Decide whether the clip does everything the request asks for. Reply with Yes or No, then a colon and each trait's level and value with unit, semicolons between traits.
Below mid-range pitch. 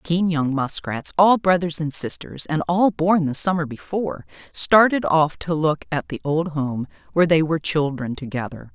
No: medium, 160 Hz